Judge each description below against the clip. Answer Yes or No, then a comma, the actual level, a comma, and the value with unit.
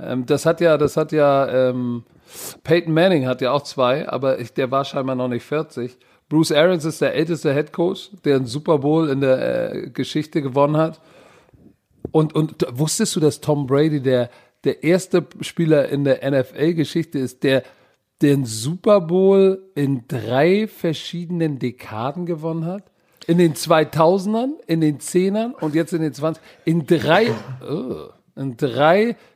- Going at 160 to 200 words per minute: Yes, average, 165 wpm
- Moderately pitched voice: Yes, medium, 155 Hz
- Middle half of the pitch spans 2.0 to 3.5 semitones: No, average, 3.9 semitones